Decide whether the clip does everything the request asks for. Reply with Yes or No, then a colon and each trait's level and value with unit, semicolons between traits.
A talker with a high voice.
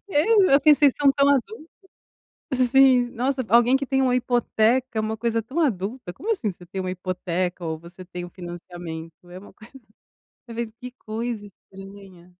Yes: high, 225 Hz